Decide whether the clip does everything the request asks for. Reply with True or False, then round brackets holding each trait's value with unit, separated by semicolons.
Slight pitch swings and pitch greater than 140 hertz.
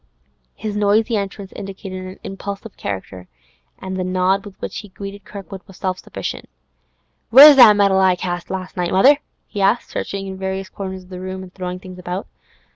True (1.4 semitones; 190 Hz)